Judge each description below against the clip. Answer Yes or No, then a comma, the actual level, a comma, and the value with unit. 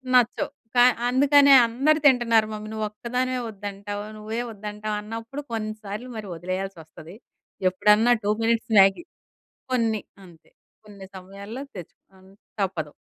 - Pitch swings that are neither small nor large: Yes, average, 3.2 semitones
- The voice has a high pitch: Yes, high, 215 Hz